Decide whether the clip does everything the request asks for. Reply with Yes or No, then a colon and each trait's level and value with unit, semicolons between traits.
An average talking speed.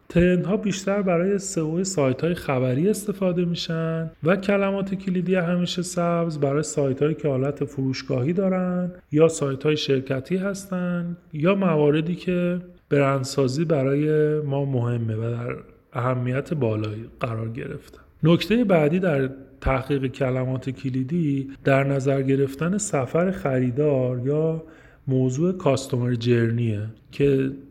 Yes: average, 120 wpm